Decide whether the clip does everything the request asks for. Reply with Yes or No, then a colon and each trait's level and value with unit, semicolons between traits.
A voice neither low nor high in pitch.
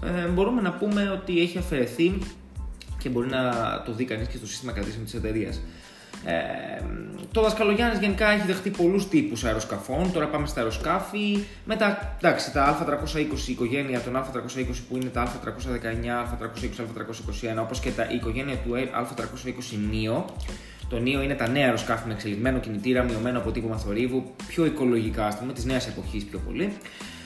No: low, 125 Hz